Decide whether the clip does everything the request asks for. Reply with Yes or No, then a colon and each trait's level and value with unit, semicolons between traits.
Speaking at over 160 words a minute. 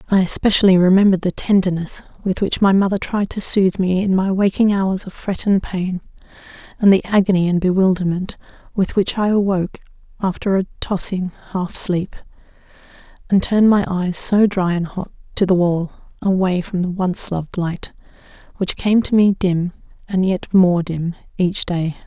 Yes: average, 170 wpm